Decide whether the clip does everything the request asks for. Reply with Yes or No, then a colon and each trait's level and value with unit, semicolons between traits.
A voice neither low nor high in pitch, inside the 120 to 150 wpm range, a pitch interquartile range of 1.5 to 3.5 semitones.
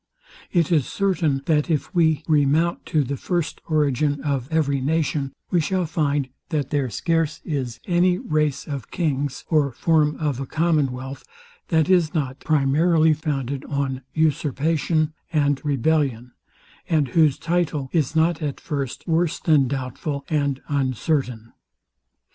Yes: medium, 150 Hz; slow, 135 wpm; average, 2.8 semitones